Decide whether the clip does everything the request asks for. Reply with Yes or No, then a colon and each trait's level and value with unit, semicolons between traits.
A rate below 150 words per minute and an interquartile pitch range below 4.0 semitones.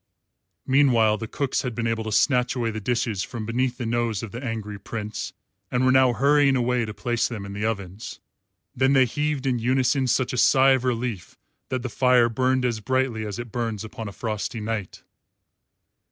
No: average, 195 wpm; average, 2.8 semitones